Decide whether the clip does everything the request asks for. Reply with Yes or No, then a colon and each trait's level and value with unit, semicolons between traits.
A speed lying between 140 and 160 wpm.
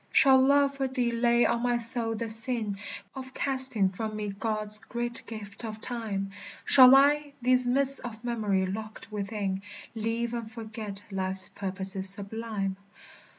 Yes: average, 150 wpm